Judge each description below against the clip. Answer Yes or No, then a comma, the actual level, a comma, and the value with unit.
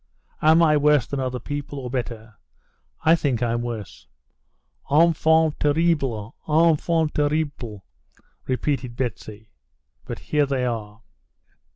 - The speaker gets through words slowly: Yes, slow, 110 wpm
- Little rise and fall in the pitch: No, average, 4.5 semitones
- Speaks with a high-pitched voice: No, medium, 140 Hz